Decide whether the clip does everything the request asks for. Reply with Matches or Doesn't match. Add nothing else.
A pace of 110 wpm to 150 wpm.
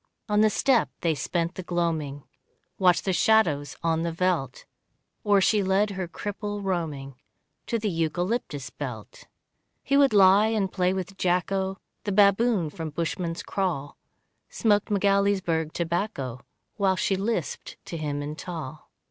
Matches